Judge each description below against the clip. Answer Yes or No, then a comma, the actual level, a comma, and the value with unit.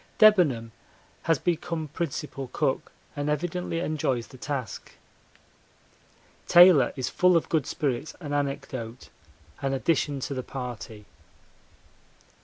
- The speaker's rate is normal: No, slow, 110 wpm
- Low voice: No, medium, 145 Hz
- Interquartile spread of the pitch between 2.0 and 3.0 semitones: No, average, 4.3 semitones